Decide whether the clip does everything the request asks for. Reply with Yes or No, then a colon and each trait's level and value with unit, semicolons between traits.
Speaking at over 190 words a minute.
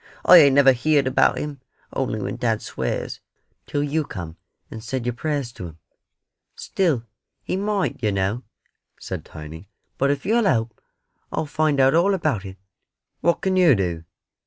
No: average, 165 wpm